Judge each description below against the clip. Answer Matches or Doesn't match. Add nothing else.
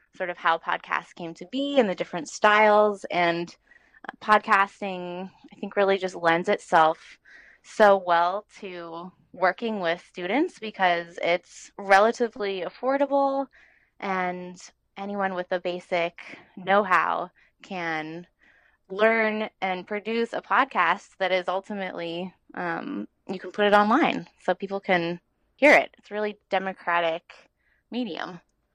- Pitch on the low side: Doesn't match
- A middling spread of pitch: Matches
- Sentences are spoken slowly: Matches